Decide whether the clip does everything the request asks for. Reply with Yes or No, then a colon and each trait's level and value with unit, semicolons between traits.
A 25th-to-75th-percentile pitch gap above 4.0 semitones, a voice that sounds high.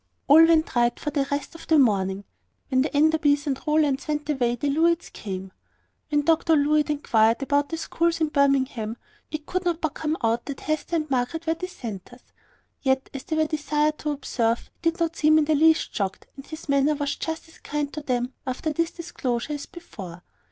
No: average, 3.5 semitones; very high, 295 Hz